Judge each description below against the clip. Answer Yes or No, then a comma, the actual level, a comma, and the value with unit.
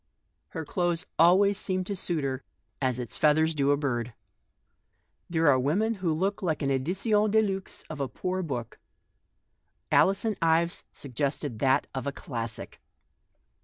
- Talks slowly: No, average, 155 wpm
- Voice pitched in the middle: Yes, medium, 160 Hz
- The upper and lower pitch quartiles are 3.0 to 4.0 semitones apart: No, average, 5.3 semitones